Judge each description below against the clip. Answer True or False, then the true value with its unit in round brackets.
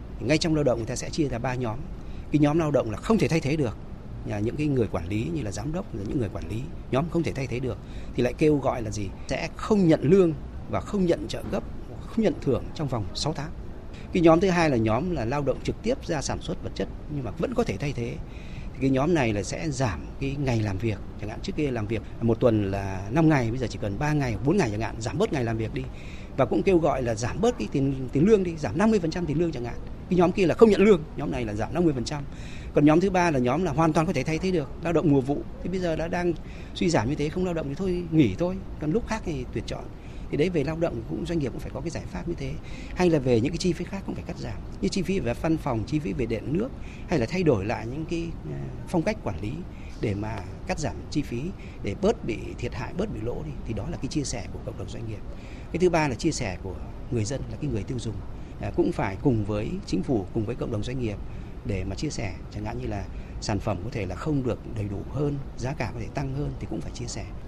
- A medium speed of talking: False (290 wpm)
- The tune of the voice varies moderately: False (6.5 semitones)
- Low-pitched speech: True (130 Hz)